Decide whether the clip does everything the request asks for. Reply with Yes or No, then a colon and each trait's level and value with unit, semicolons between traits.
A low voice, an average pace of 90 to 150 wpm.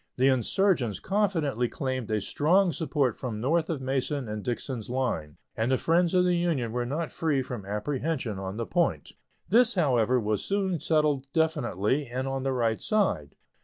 No: low, 130 Hz; average, 170 wpm